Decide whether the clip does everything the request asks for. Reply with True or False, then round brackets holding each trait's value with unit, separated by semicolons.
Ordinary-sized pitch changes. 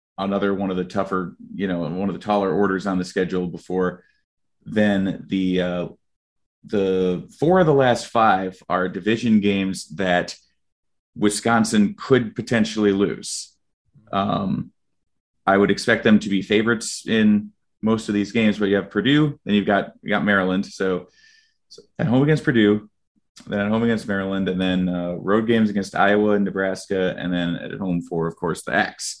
True (3.1 semitones)